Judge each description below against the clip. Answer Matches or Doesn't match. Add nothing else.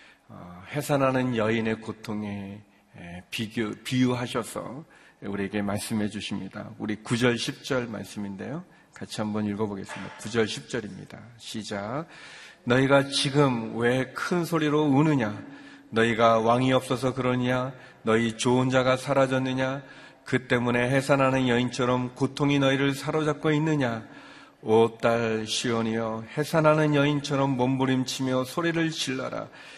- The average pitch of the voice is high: Doesn't match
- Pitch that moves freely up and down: Doesn't match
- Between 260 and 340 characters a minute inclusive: Matches